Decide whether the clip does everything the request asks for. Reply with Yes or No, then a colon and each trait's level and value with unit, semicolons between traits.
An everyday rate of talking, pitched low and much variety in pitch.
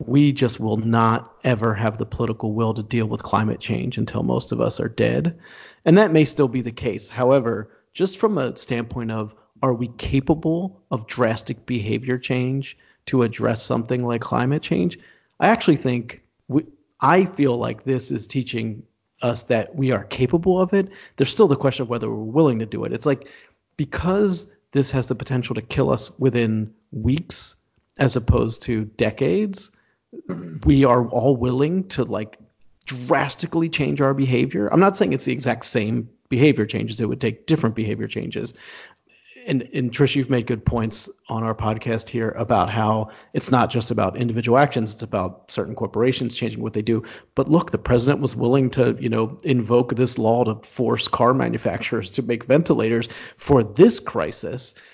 No: average, 180 wpm; low, 125 Hz; average, 3.5 semitones